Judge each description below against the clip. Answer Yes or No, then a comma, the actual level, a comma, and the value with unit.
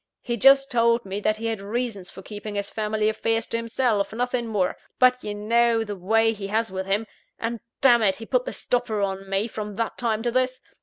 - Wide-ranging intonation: No, narrow, 2.5 semitones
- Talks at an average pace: No, fast, 220 wpm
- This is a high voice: Yes, high, 225 Hz